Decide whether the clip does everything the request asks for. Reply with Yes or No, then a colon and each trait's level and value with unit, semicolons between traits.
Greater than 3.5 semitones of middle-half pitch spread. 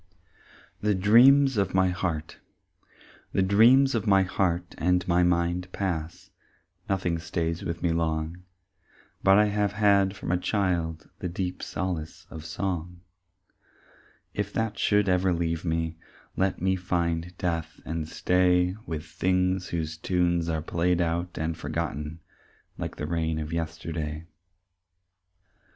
No: narrow, 2.4 semitones